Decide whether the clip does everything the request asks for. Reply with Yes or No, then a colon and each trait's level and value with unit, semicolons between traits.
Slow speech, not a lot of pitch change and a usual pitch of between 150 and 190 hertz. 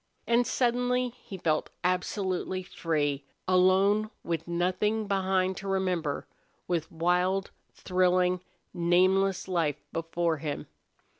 Yes: slow, 100 wpm; narrow, 2.2 semitones; medium, 185 Hz